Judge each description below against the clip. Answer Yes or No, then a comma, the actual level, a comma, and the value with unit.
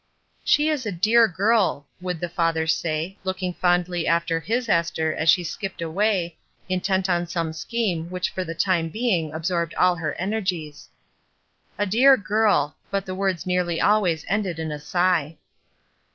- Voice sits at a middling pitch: Yes, medium, 180 Hz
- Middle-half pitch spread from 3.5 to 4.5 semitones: No, average, 3.1 semitones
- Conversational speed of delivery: Yes, average, 160 wpm